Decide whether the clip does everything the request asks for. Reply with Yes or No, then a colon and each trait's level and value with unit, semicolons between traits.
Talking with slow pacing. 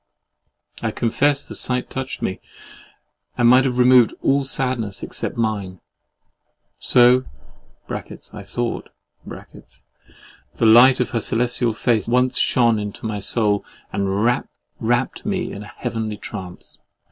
Yes: slow, 125 wpm